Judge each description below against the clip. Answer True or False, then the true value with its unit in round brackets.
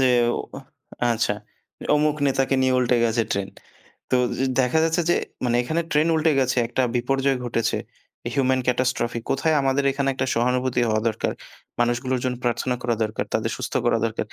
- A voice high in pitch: False (130 Hz)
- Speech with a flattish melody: True (2.2 semitones)